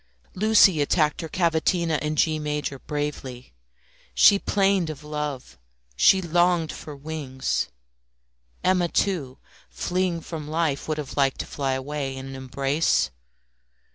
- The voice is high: No, medium, 150 Hz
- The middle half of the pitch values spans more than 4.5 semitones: No, average, 3.6 semitones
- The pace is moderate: No, slow, 130 wpm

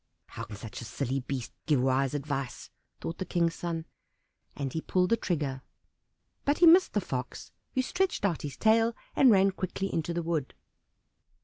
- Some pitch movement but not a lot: No, wide, 6.2 semitones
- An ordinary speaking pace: Yes, average, 180 wpm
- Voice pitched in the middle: Yes, medium, 165 Hz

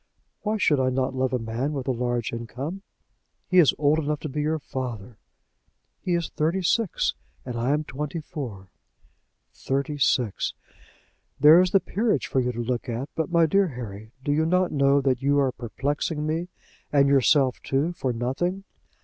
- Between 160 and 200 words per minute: Yes, average, 180 wpm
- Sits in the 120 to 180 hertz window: Yes, medium, 140 Hz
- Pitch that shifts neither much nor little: Yes, average, 4.1 semitones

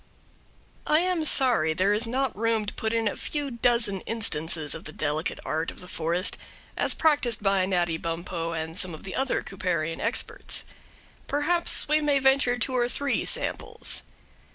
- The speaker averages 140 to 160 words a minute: No, average, 170 wpm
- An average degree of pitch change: No, wide, 7.6 semitones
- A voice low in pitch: No, high, 210 Hz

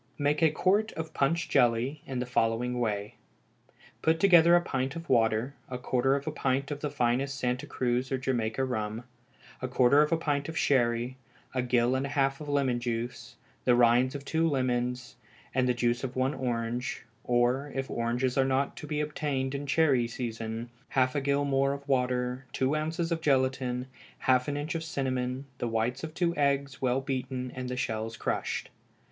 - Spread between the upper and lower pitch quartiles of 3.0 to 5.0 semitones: No, narrow, 2.6 semitones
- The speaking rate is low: No, average, 190 wpm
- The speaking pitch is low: Yes, low, 130 Hz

